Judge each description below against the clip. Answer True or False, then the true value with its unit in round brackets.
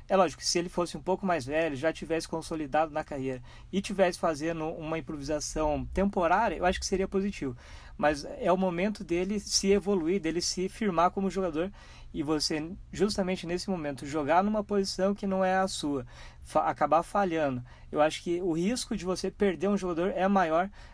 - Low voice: False (175 Hz)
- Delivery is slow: False (185 wpm)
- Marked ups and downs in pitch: False (3.6 semitones)